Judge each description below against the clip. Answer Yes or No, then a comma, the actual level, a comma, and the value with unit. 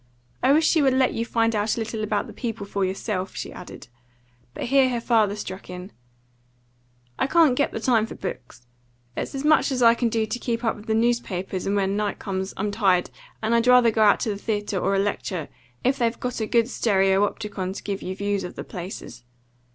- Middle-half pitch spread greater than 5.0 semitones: No, average, 3.3 semitones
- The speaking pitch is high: Yes, high, 215 Hz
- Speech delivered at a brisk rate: Yes, fast, 220 wpm